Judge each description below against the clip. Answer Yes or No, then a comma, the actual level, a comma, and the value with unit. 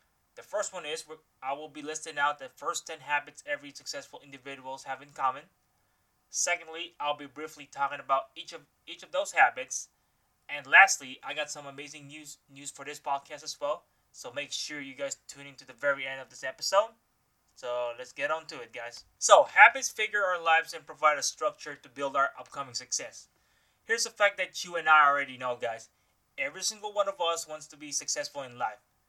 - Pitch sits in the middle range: Yes, medium, 150 Hz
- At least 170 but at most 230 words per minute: Yes, fast, 205 wpm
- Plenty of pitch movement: No, average, 3.6 semitones